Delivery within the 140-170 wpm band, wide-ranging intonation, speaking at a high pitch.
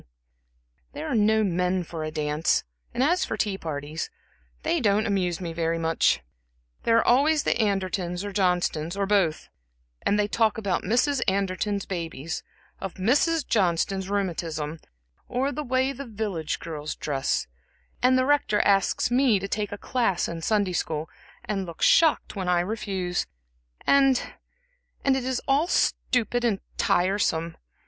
Yes: average, 155 wpm; wide, 5.8 semitones; high, 200 Hz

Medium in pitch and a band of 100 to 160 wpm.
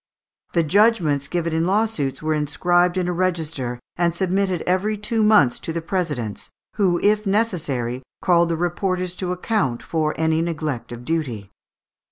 Yes: medium, 170 Hz; average, 155 wpm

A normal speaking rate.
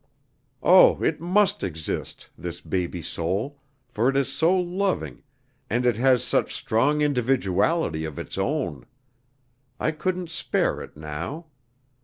No: slow, 130 wpm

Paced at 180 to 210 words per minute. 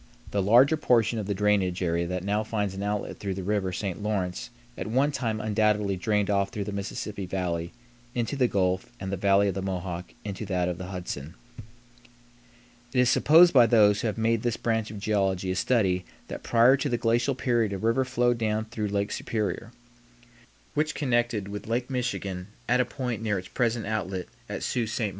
Yes: average, 200 wpm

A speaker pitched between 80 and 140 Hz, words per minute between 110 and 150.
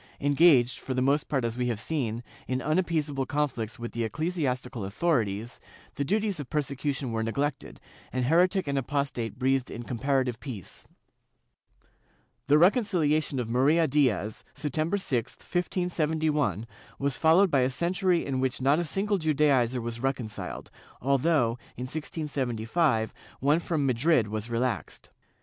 Yes: low, 135 Hz; average, 140 wpm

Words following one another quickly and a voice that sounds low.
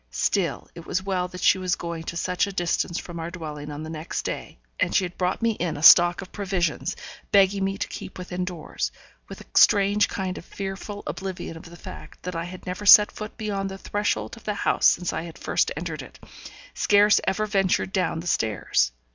No: fast, 215 wpm; medium, 180 Hz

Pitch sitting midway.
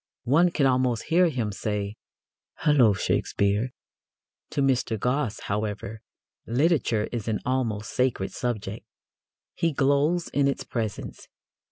No: low, 125 Hz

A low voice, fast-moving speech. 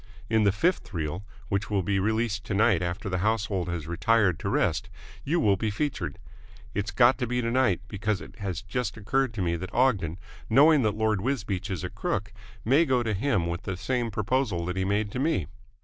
Yes: low, 105 Hz; fast, 210 wpm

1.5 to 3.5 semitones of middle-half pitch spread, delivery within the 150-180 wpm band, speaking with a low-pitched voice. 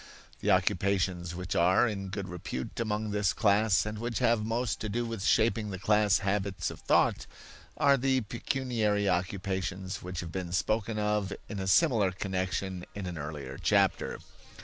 Yes: average, 2.8 semitones; average, 165 wpm; low, 100 Hz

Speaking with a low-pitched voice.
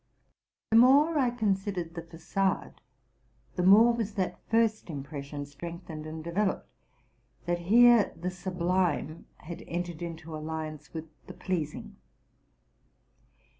No: medium, 175 Hz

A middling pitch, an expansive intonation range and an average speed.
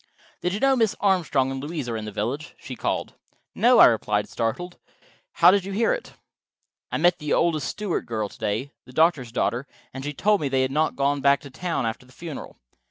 No: medium, 145 Hz; wide, 5.9 semitones; fast, 220 wpm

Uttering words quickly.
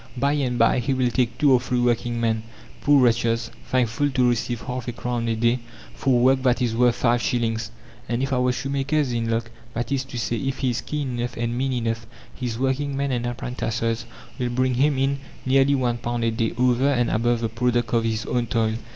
Yes: fast, 220 wpm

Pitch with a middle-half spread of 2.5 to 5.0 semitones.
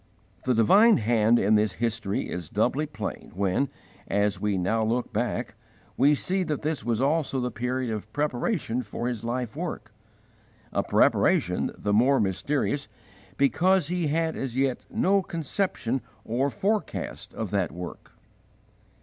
No: wide, 5.6 semitones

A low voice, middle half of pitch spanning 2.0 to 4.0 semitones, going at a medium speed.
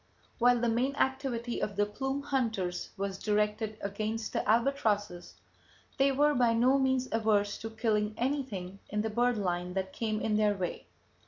No: high, 220 Hz; average, 3.4 semitones; average, 165 wpm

